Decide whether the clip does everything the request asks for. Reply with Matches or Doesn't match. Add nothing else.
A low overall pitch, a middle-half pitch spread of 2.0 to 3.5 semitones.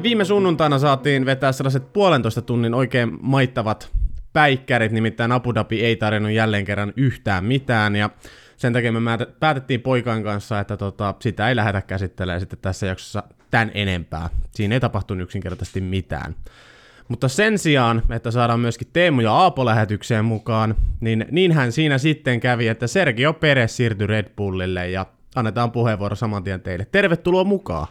Doesn't match